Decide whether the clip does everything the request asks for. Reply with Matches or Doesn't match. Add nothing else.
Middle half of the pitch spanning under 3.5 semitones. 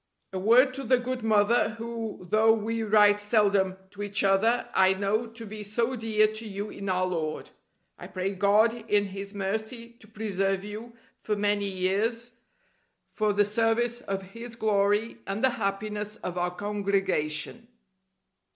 Matches